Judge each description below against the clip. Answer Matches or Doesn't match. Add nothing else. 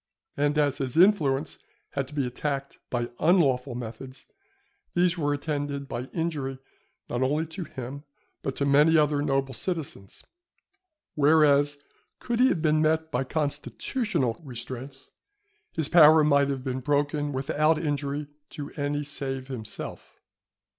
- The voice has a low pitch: Doesn't match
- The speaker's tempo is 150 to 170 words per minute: Doesn't match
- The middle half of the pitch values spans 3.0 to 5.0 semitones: Doesn't match